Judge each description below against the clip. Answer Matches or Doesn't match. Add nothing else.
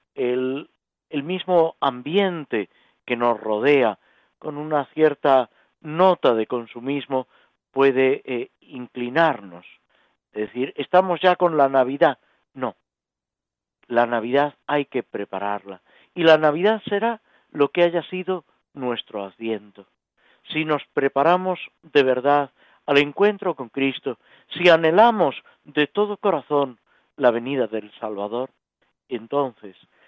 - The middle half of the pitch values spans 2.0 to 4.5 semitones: Doesn't match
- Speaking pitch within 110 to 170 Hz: Matches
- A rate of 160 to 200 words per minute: Doesn't match